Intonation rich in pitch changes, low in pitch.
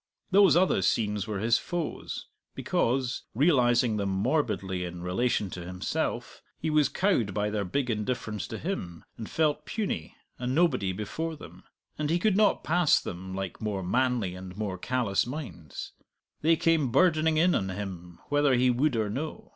Yes: wide, 8.0 semitones; low, 120 Hz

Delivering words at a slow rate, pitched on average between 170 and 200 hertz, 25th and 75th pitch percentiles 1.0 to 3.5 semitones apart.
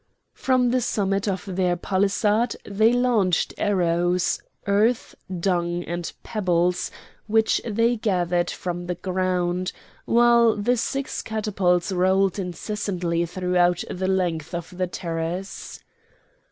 Yes: slow, 115 wpm; medium, 185 Hz; average, 3.2 semitones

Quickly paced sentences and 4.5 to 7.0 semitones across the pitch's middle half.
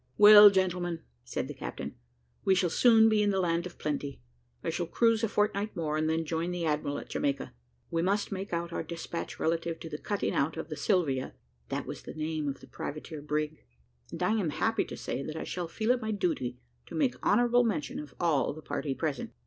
Yes: fast, 220 wpm; average, 5.1 semitones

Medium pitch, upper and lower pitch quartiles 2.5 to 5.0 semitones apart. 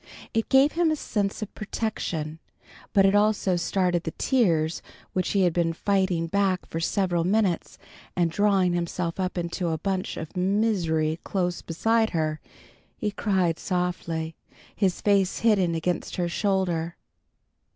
Yes: medium, 180 Hz; average, 3.2 semitones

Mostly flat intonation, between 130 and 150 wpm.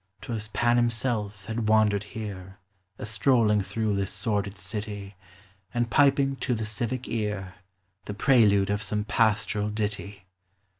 Yes: narrow, 2.1 semitones; average, 140 wpm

